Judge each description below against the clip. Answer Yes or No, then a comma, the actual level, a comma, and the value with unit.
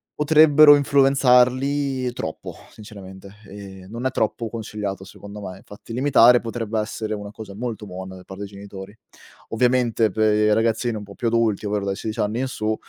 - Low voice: Yes, low, 110 Hz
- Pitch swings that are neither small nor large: Yes, average, 3.5 semitones